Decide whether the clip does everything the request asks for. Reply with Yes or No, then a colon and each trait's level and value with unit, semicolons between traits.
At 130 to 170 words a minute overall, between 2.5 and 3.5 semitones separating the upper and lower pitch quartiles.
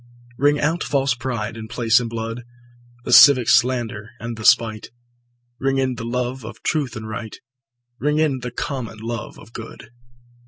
Yes: average, 165 wpm; average, 2.8 semitones